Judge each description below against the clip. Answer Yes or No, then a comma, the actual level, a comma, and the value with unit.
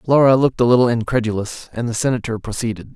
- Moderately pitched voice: No, low, 120 Hz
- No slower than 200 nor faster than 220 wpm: No, average, 185 wpm